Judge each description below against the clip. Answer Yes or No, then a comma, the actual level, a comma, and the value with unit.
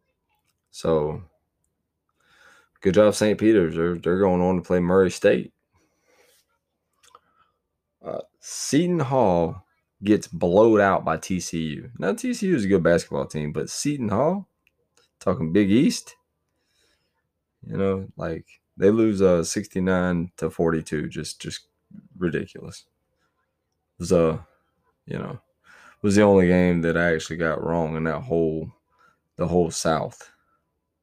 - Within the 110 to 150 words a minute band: Yes, slow, 135 wpm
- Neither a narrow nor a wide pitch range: Yes, average, 3.4 semitones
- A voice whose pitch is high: No, very low, 90 Hz